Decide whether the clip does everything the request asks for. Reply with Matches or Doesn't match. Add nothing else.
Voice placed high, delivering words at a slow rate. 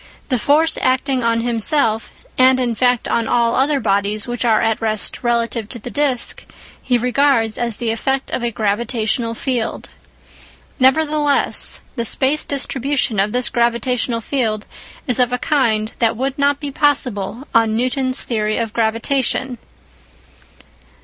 Doesn't match